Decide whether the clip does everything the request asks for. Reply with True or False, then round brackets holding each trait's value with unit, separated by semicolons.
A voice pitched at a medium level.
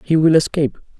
True (155 Hz)